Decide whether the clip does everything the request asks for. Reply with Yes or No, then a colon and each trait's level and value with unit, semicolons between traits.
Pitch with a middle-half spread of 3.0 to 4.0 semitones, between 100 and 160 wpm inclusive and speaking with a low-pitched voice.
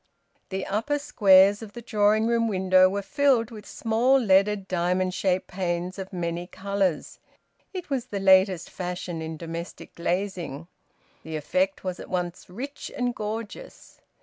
No: average, 3.3 semitones; average, 150 wpm; high, 190 Hz